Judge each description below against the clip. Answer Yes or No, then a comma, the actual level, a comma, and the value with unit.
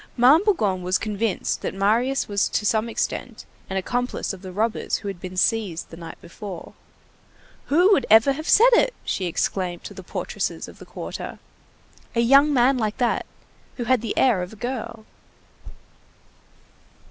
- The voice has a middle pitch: No, high, 225 Hz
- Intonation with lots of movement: No, average, 4.9 semitones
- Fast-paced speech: No, average, 170 wpm